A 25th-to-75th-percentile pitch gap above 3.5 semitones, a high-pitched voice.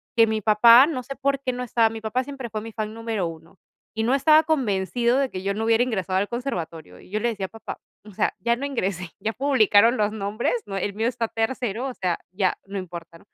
Yes: average, 4.0 semitones; high, 225 Hz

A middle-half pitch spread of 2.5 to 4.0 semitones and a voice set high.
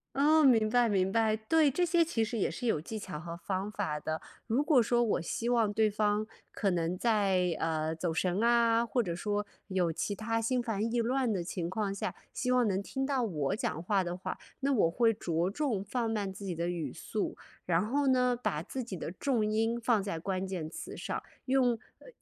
No: average, 4.6 semitones; high, 215 Hz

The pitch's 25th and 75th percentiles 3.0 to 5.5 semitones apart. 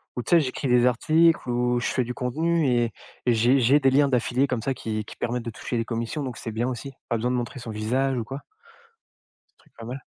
No: narrow, 2.5 semitones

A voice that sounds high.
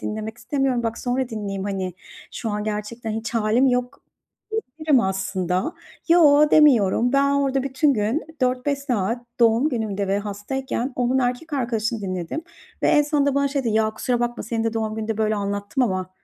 Yes: high, 235 Hz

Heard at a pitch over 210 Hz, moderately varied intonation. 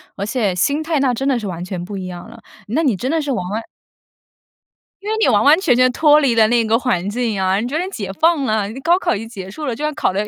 No: high, 235 Hz; wide, 6.4 semitones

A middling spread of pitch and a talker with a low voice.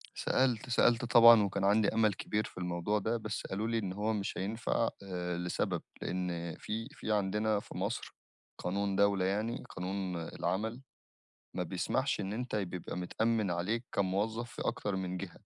Yes: average, 3.3 semitones; low, 100 Hz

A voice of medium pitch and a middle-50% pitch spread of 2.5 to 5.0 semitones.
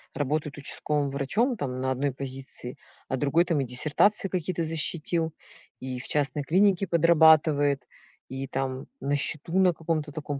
Yes: medium, 150 Hz; average, 3.4 semitones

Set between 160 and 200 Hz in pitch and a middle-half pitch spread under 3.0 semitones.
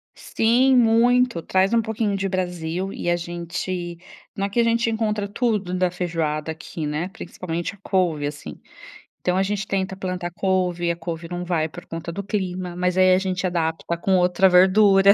Yes: medium, 185 Hz; narrow, 2.4 semitones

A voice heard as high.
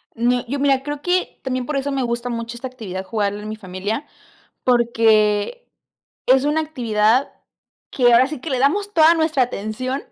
Yes: very high, 250 Hz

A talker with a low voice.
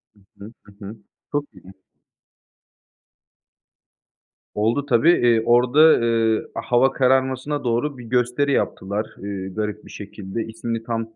Yes: low, 115 Hz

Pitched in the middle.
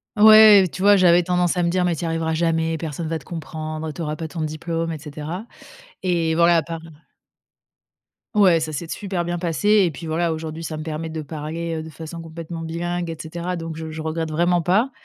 Yes: medium, 165 Hz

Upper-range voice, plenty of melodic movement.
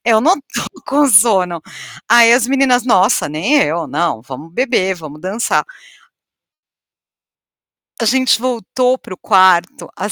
Yes: high, 210 Hz; wide, 6.3 semitones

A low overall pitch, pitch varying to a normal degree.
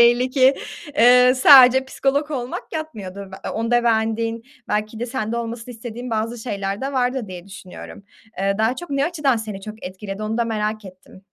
No: high, 230 Hz; average, 3.0 semitones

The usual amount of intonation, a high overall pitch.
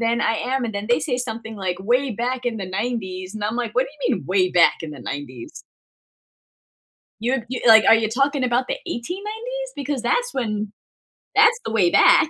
Yes: average, 4.2 semitones; high, 235 Hz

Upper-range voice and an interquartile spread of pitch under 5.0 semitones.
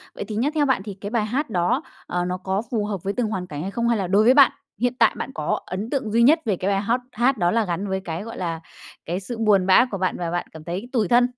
Yes: high, 205 Hz; average, 4.4 semitones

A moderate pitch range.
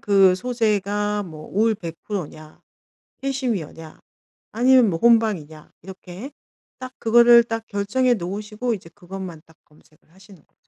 Yes: average, 4.7 semitones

